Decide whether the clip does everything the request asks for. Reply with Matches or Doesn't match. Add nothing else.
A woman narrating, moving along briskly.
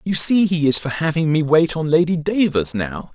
Doesn't match